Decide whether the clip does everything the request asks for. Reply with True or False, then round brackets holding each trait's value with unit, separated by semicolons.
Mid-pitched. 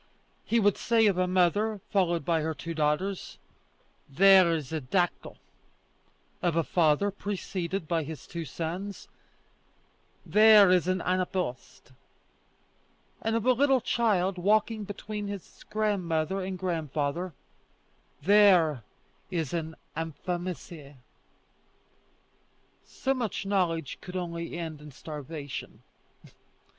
True (180 Hz)